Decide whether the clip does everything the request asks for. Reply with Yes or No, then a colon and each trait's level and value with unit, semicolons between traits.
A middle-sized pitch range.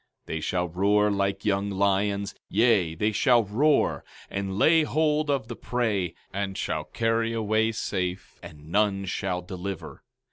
Yes: average, 3.0 semitones